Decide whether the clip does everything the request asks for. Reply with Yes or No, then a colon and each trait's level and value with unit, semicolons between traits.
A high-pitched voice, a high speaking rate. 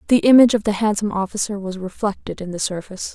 Yes: high, 205 Hz; fast, 210 wpm